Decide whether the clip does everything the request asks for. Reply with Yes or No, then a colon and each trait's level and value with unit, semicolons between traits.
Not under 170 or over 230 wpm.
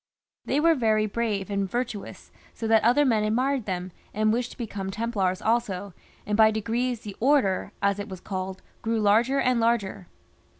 Yes: average, 180 wpm